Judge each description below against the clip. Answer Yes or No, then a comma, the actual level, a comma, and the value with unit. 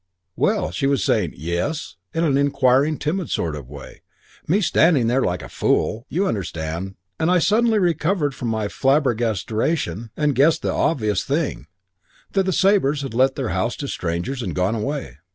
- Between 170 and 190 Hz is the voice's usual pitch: No, low, 135 Hz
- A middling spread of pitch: No, wide, 7.4 semitones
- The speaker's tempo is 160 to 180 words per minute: Yes, average, 170 wpm